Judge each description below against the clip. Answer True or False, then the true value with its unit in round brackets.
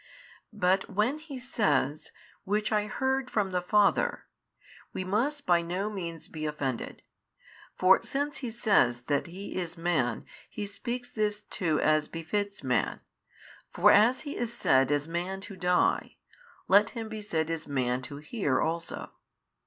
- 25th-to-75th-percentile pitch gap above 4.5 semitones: True (5.6 semitones)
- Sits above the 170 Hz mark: True (190 Hz)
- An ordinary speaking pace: True (155 wpm)